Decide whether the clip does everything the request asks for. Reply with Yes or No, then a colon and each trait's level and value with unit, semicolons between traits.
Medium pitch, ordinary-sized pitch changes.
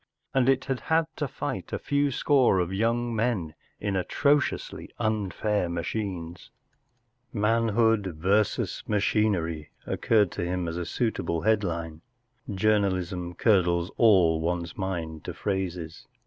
No: low, 100 Hz; average, 4.6 semitones